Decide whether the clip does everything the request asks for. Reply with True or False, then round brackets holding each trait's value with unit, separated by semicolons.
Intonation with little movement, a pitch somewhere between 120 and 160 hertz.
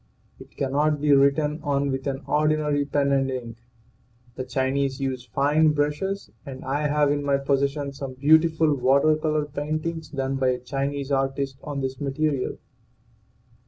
True (1.8 semitones; 140 Hz)